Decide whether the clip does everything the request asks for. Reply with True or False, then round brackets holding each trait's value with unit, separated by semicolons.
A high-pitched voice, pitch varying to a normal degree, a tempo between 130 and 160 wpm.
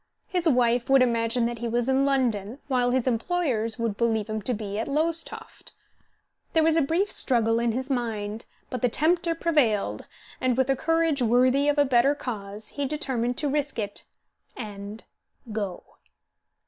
False (245 Hz; 4.1 semitones; 170 wpm)